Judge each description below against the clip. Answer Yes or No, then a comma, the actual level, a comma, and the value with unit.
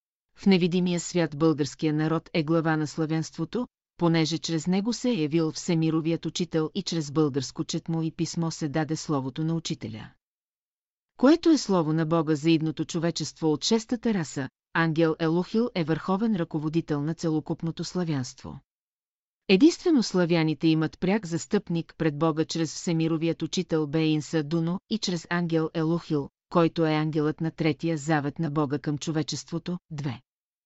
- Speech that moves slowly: No, average, 145 wpm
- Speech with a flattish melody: Yes, narrow, 1.8 semitones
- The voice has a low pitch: No, medium, 165 Hz